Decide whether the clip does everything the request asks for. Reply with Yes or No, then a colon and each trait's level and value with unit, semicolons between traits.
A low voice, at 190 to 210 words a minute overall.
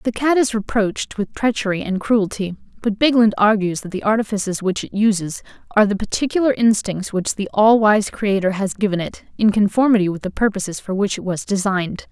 No: high, 205 Hz; average, 195 wpm